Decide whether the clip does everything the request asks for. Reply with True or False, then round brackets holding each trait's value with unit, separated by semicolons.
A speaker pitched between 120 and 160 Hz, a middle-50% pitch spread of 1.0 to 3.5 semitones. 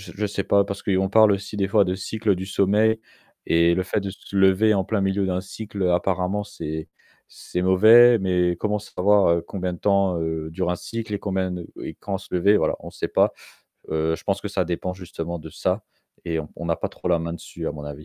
False (95 Hz; 2.5 semitones)